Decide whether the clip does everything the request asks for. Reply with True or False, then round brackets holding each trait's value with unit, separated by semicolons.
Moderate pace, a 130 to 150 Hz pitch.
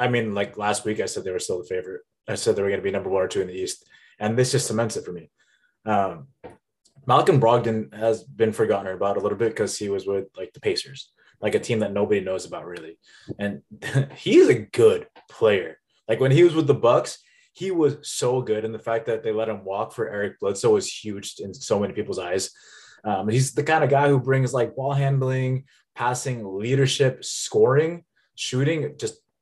False (220 wpm; 135 Hz)